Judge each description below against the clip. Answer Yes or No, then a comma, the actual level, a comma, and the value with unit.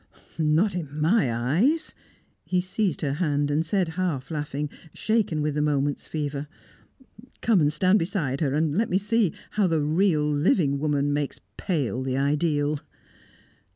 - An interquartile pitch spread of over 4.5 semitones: No, average, 4.1 semitones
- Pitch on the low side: No, medium, 150 Hz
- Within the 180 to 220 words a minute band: No, average, 155 wpm